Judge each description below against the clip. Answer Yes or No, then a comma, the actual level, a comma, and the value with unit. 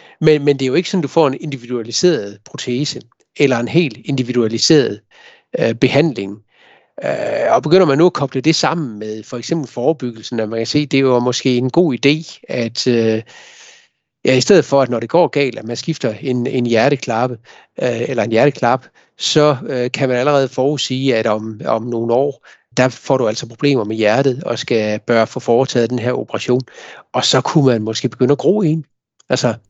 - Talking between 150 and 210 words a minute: Yes, average, 200 wpm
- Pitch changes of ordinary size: Yes, average, 3.6 semitones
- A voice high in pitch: No, low, 130 Hz